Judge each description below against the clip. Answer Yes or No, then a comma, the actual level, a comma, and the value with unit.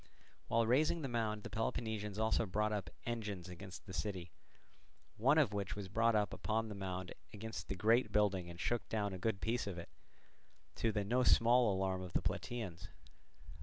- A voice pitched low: Yes, low, 105 Hz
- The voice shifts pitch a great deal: No, average, 3.1 semitones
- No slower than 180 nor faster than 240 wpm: Yes, average, 185 wpm